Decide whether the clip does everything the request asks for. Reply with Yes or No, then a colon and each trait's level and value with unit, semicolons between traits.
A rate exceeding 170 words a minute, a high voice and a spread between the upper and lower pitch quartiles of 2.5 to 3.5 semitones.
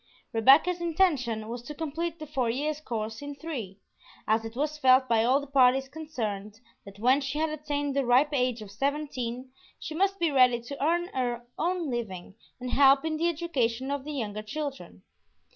No: average, 185 wpm; very high, 270 Hz; average, 4.3 semitones